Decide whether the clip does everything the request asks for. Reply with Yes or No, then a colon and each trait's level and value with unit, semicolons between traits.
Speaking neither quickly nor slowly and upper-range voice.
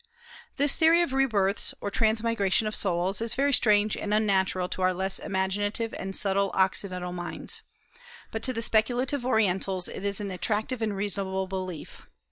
Yes: average, 165 wpm; high, 200 Hz